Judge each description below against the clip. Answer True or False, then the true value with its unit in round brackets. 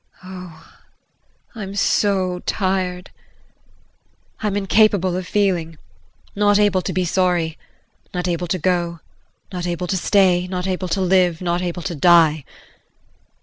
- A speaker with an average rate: False (130 wpm)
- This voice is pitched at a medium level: True (180 Hz)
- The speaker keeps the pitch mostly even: True (1.6 semitones)